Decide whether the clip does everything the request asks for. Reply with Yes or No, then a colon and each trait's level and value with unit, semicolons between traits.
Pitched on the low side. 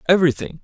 No: medium, 155 Hz